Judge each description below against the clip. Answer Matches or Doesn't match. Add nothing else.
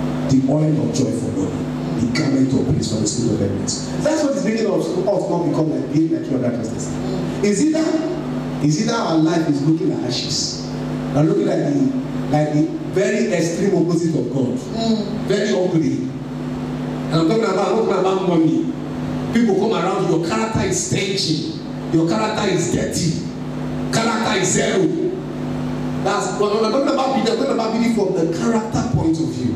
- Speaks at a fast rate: Matches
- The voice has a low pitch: Doesn't match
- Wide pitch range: Matches